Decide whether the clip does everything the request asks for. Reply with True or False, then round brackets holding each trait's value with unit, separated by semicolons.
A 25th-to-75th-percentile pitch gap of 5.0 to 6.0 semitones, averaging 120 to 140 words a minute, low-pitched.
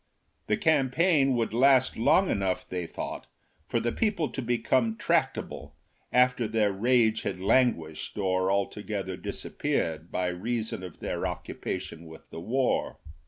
True (5.3 semitones; 135 wpm; 110 Hz)